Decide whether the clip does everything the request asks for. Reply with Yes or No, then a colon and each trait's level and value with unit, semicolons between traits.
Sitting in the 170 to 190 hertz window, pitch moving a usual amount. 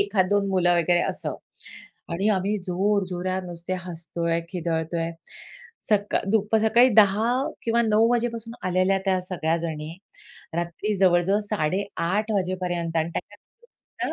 Yes: medium, 185 Hz; average, 3.4 semitones